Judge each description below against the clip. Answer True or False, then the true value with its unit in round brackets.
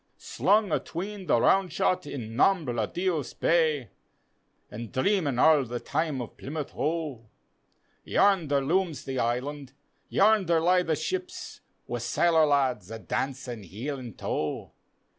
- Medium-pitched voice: True (145 Hz)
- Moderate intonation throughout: False (5.7 semitones)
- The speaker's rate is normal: False (130 wpm)